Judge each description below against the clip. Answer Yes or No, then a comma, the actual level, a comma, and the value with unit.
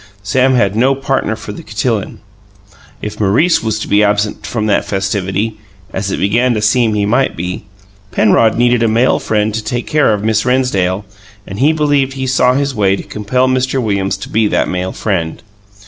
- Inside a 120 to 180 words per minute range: No, average, 195 wpm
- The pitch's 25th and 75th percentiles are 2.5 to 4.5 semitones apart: Yes, average, 3.9 semitones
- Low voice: Yes, low, 110 Hz